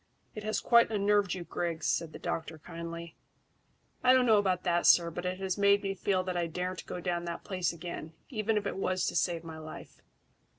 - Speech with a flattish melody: No, average, 3.0 semitones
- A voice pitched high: No, medium, 180 Hz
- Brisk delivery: Yes, fast, 215 wpm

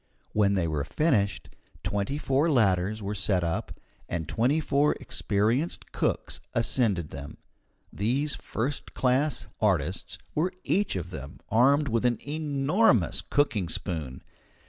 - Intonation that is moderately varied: No, wide, 7.0 semitones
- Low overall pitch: Yes, low, 115 Hz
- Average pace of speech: No, slow, 125 wpm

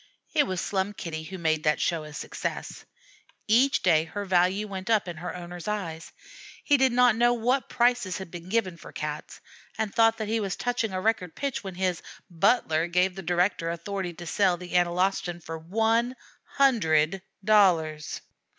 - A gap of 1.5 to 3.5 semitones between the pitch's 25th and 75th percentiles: No, average, 4.5 semitones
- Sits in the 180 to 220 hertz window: Yes, medium, 185 Hz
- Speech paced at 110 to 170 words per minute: No, average, 180 wpm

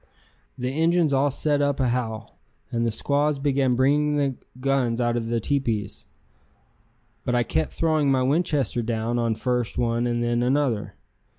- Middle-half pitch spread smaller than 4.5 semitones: Yes, average, 3.3 semitones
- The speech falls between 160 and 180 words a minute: Yes, average, 165 wpm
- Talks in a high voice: No, low, 125 Hz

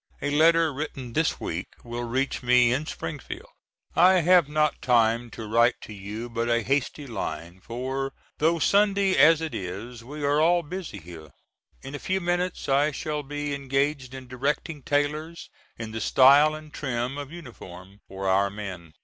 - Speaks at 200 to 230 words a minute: No, average, 170 wpm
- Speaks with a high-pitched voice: No, low, 135 Hz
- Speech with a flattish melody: No, average, 4.7 semitones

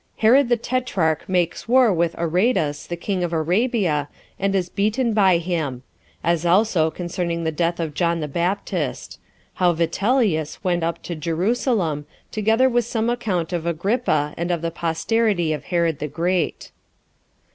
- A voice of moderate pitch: Yes, medium, 175 Hz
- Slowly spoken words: No, average, 155 wpm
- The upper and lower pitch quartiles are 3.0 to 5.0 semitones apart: Yes, average, 4.6 semitones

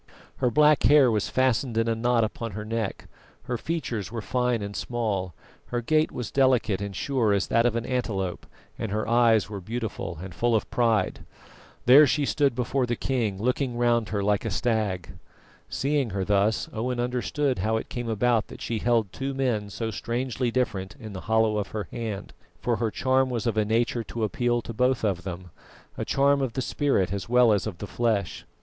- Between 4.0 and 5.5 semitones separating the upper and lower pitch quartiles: No, average, 3.1 semitones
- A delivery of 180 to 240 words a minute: Yes, average, 200 wpm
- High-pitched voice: No, low, 115 Hz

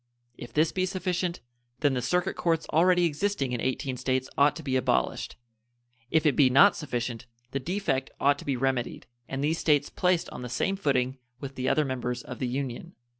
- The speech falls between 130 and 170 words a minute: No, average, 195 wpm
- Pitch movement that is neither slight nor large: Yes, average, 4.6 semitones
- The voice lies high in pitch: No, medium, 140 Hz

